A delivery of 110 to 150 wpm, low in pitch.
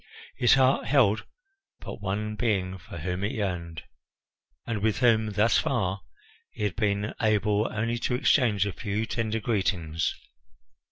Yes: average, 145 wpm; low, 105 Hz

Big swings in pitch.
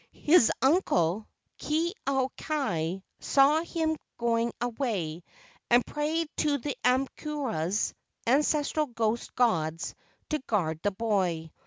Yes: wide, 7.5 semitones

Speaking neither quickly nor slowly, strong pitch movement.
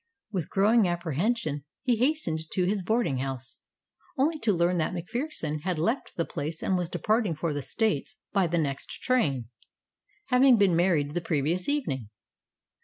Yes: average, 160 wpm; wide, 6.6 semitones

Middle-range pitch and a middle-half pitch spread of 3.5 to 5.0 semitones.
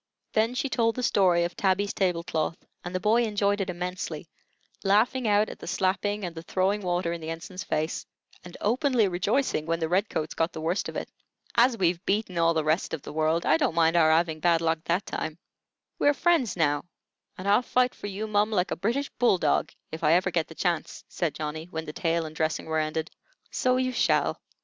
Yes: medium, 180 Hz; average, 4.2 semitones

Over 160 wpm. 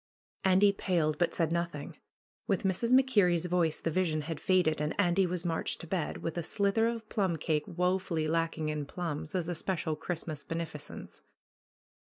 Yes: average, 170 wpm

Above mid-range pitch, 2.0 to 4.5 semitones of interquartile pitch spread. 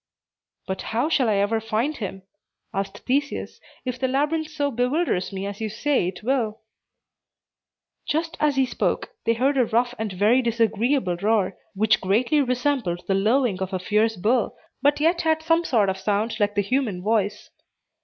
No: high, 230 Hz; average, 5.2 semitones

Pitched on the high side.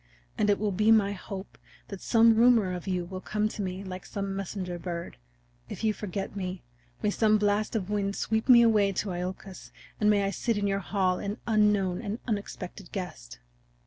Yes: high, 200 Hz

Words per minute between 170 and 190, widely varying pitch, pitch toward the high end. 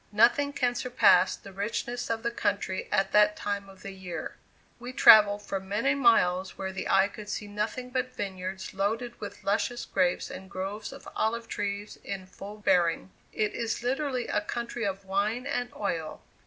No: average, 175 wpm; average, 3.5 semitones; high, 205 Hz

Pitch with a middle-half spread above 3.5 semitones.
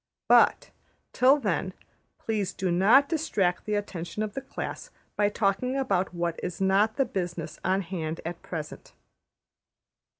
Yes: average, 3.9 semitones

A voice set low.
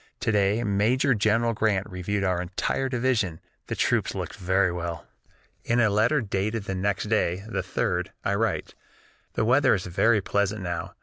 Yes: low, 100 Hz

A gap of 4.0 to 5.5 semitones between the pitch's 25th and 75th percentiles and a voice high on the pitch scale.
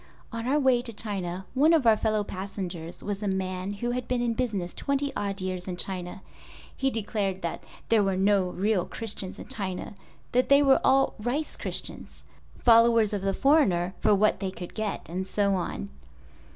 Yes: average, 4.3 semitones; high, 205 Hz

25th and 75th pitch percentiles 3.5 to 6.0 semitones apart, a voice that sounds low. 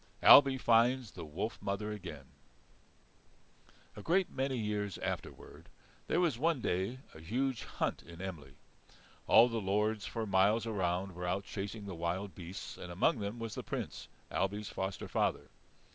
Yes: average, 3.8 semitones; low, 100 Hz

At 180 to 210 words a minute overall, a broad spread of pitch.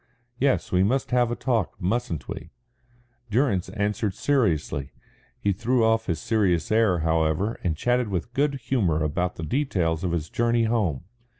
No: average, 160 wpm; wide, 6.0 semitones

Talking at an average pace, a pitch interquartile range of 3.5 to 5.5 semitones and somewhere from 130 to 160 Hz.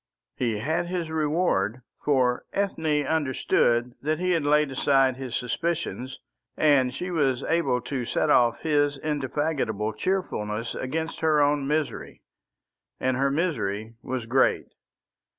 No: slow, 130 wpm; average, 4.2 semitones; medium, 140 Hz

